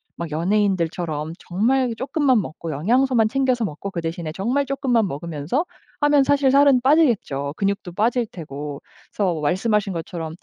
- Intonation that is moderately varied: No, wide, 7.8 semitones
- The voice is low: No, high, 200 Hz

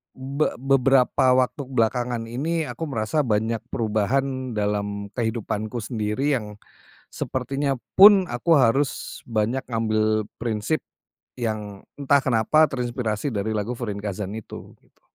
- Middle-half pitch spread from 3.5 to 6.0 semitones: Yes, average, 3.8 semitones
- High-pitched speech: No, low, 120 Hz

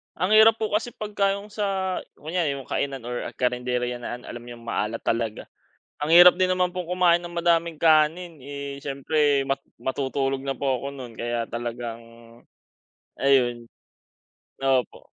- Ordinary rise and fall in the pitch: No, wide, 6.4 semitones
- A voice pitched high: No, medium, 140 Hz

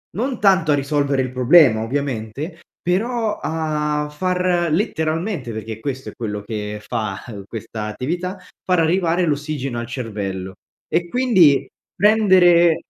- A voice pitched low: No, medium, 150 Hz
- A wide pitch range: Yes, wide, 7.1 semitones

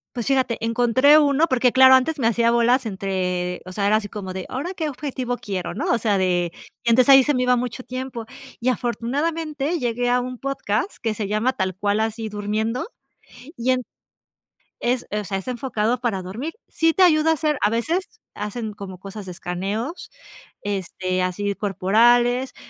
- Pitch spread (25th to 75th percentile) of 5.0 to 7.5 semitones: No, average, 4.2 semitones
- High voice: Yes, high, 235 Hz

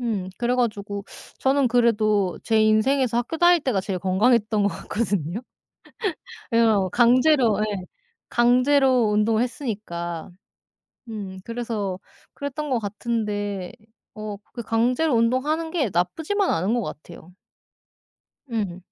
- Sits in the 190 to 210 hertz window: No, high, 225 Hz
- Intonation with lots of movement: No, average, 3.8 semitones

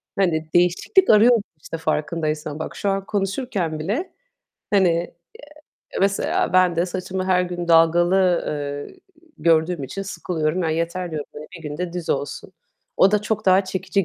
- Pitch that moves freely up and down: No, average, 3.2 semitones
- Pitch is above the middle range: No, medium, 175 Hz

